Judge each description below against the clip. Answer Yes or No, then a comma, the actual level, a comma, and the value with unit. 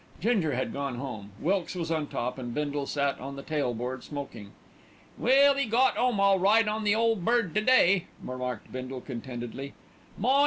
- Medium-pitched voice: Yes, medium, 150 Hz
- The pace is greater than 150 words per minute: Yes, average, 185 wpm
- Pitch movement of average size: No, wide, 8.8 semitones